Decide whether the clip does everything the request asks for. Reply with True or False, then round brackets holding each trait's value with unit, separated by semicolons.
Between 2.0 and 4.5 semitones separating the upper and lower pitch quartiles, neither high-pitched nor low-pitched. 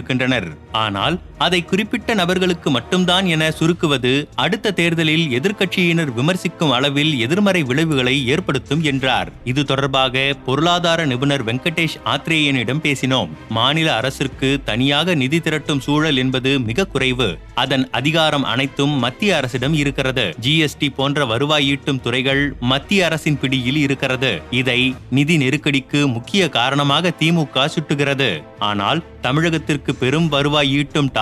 True (3.6 semitones; 145 Hz)